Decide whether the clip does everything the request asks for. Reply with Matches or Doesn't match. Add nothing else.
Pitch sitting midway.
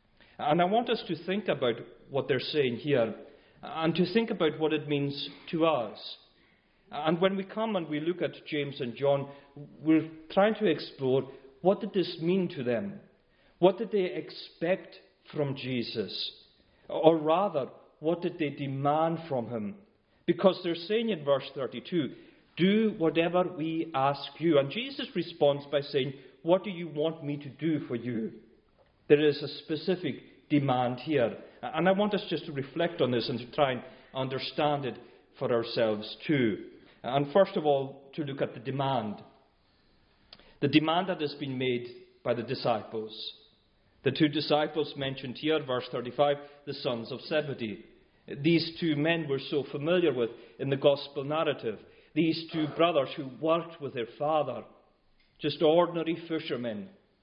Matches